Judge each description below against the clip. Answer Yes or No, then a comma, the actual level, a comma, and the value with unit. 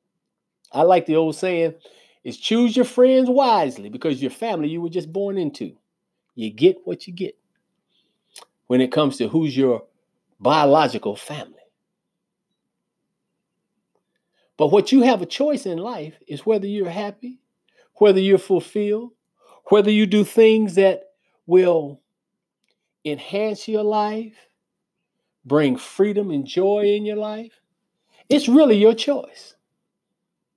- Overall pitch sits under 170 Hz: No, high, 200 Hz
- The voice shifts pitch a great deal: No, average, 4.8 semitones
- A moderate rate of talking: No, slow, 130 wpm